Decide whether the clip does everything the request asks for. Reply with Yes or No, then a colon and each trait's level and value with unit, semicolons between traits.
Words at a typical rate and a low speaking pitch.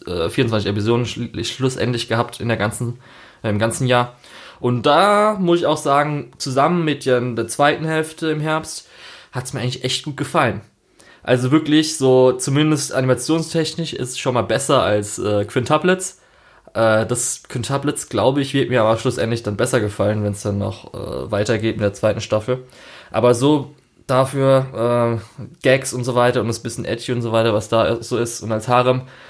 Yes: average, 180 wpm; low, 125 Hz